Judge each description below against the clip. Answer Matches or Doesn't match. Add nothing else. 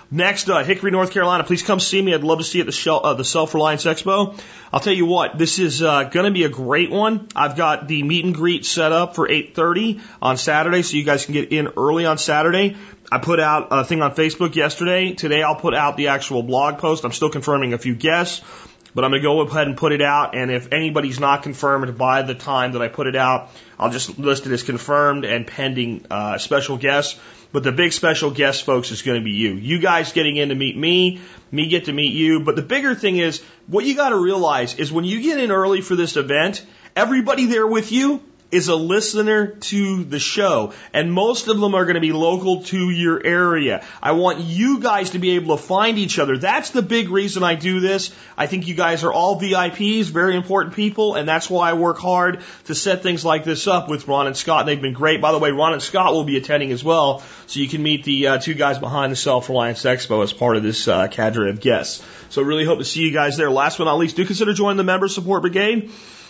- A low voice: Doesn't match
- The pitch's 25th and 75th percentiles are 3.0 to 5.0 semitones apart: Matches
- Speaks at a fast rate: Matches